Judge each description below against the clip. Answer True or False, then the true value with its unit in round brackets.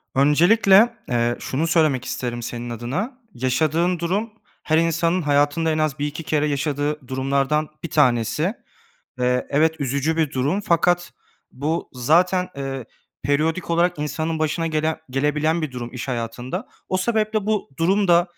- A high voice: False (155 Hz)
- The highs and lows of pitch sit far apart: False (4.1 semitones)